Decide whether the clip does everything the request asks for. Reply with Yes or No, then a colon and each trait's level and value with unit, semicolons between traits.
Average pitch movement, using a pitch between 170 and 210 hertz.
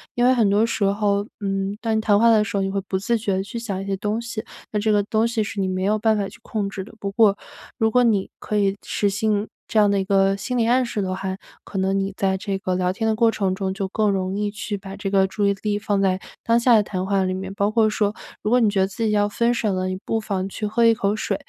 No: narrow, 2.1 semitones; high, 205 Hz